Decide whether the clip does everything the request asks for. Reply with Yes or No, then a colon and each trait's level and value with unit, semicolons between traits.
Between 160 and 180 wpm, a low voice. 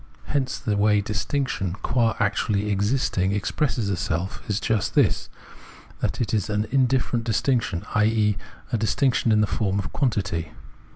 No: average, 140 wpm; low, 105 Hz